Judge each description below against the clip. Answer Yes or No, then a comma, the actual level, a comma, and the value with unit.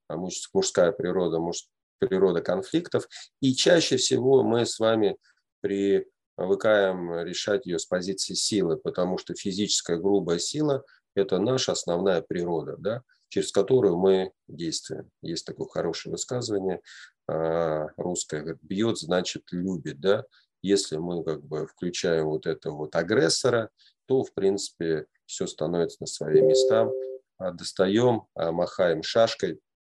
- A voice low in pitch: Yes, very low, 95 Hz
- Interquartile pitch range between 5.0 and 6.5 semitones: Yes, wide, 5.6 semitones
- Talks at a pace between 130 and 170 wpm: No, average, 120 wpm